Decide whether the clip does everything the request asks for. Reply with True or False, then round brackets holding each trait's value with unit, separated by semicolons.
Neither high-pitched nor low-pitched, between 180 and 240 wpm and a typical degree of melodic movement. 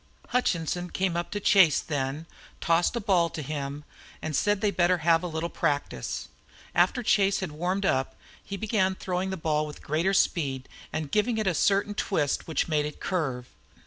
True (175 Hz; 185 wpm; 4.2 semitones)